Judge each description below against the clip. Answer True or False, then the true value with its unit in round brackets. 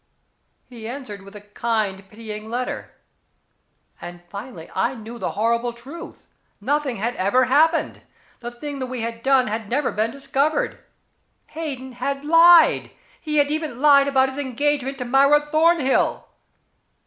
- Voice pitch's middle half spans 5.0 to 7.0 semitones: False (4.1 semitones)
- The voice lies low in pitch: False (255 Hz)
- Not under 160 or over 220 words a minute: False (140 wpm)